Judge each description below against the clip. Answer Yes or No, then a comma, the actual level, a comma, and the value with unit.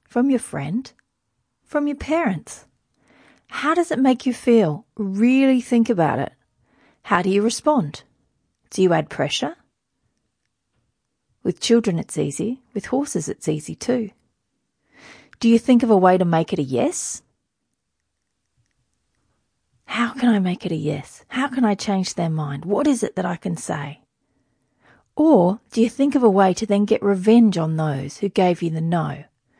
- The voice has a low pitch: No, high, 205 Hz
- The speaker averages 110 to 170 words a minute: Yes, average, 165 wpm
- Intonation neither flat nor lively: No, wide, 7.0 semitones